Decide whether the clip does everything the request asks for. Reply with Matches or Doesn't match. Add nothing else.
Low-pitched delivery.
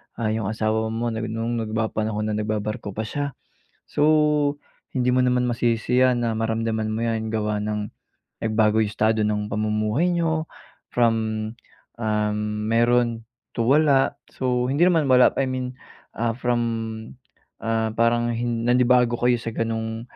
Matches